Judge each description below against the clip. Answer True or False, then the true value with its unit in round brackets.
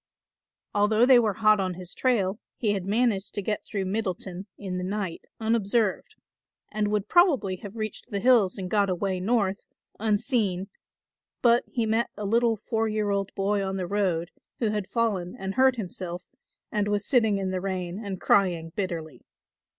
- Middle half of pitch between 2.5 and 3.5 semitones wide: True (2.8 semitones)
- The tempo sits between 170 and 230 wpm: True (175 wpm)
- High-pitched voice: True (205 Hz)